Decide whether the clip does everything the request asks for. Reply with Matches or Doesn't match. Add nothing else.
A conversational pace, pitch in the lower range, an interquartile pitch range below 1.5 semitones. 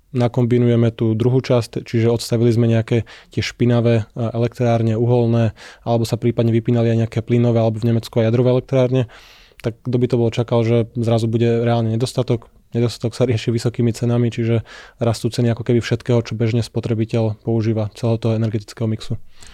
Doesn't match